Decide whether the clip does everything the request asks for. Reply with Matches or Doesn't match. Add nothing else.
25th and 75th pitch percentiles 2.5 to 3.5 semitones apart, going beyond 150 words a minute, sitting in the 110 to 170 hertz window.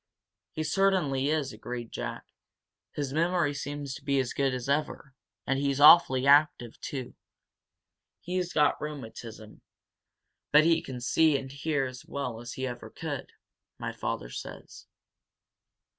Doesn't match